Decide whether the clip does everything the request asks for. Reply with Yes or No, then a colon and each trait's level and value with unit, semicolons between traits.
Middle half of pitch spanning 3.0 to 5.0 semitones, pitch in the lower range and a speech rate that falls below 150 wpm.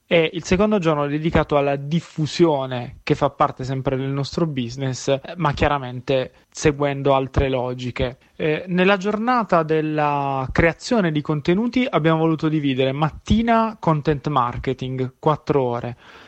No: average, 3.7 semitones; medium, 150 Hz; average, 130 wpm